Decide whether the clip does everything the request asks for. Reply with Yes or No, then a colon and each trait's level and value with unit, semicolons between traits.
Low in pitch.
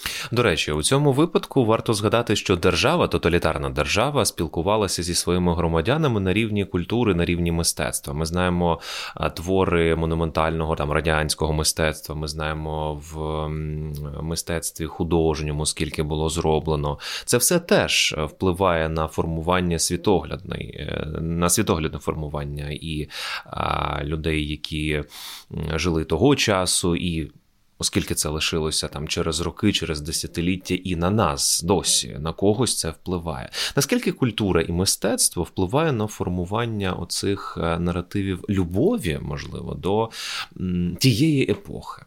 Yes: very low, 85 Hz